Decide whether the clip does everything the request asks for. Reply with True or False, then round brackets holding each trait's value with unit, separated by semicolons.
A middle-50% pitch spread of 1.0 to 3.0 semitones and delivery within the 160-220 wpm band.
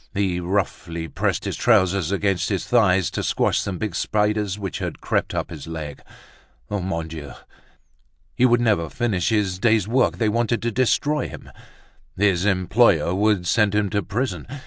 False (3.6 semitones; 165 wpm)